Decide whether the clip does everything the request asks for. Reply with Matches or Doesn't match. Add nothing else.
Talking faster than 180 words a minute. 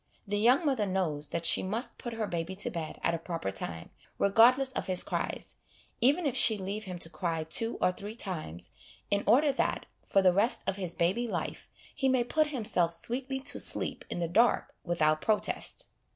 Matches